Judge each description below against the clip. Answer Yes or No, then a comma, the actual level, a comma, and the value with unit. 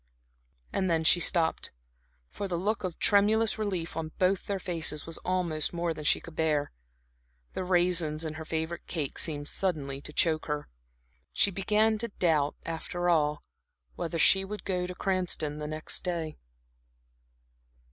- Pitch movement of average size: Yes, average, 3.1 semitones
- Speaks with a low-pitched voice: No, medium, 170 Hz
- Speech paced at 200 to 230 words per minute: No, average, 155 wpm